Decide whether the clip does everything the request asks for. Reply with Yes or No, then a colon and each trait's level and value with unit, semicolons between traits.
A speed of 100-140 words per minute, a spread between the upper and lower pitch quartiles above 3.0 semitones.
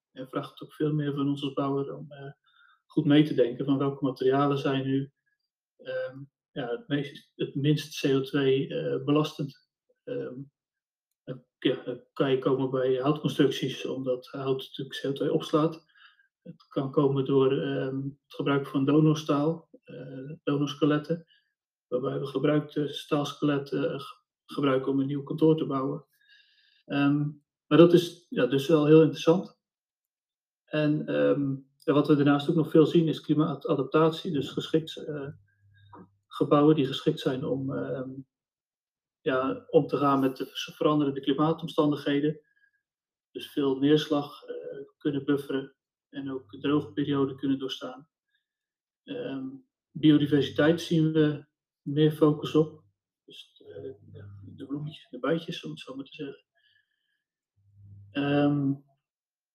No: slow, 135 wpm; narrow, 2.6 semitones